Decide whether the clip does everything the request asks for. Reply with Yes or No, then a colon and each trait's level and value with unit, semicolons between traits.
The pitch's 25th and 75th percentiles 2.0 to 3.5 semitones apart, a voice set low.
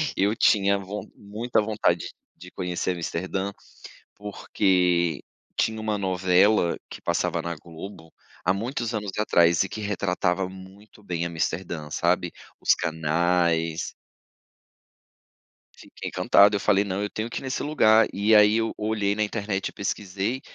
Yes: average, 3.2 semitones; very low, 95 Hz